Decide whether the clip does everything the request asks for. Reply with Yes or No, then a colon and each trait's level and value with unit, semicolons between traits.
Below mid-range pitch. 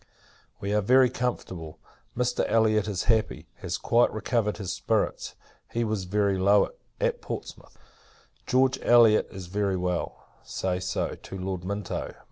Yes: low, 105 Hz